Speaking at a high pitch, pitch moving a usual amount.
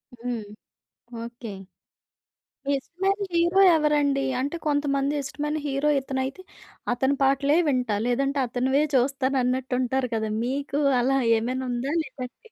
No: very high, 270 Hz; narrow, 2.3 semitones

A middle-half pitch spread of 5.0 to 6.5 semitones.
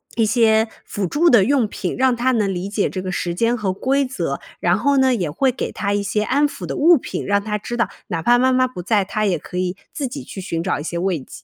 Yes: wide, 5.6 semitones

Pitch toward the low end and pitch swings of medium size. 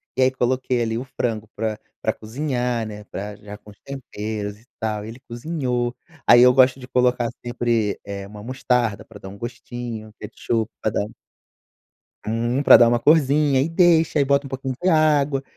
Yes: low, 120 Hz; average, 3.4 semitones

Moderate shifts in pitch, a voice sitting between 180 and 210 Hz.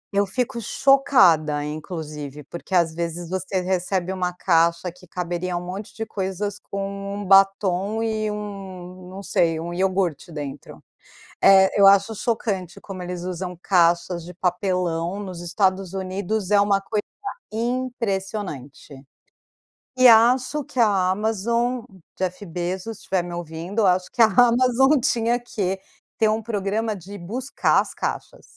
Yes: average, 3.4 semitones; high, 190 Hz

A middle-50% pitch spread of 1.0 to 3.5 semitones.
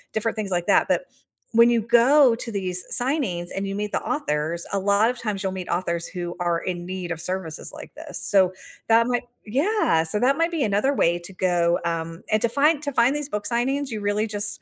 No: wide, 5.4 semitones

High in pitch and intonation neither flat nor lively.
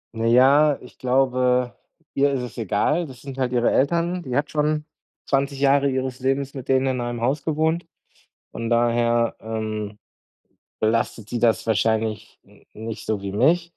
No: low, 130 Hz; average, 3.3 semitones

